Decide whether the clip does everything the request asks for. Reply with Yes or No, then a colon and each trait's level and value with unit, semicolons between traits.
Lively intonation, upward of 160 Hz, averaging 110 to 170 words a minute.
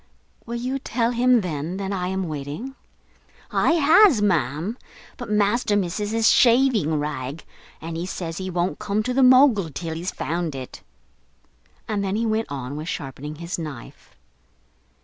Yes: wide, 6.7 semitones; high, 190 Hz; average, 160 wpm